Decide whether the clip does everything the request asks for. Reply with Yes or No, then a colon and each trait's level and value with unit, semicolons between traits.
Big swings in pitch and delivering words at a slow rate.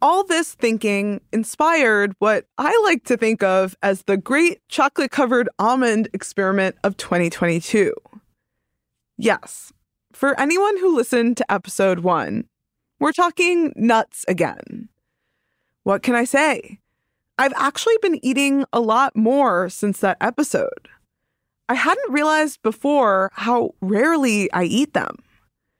Yes: wide, 6.6 semitones; slow, 125 wpm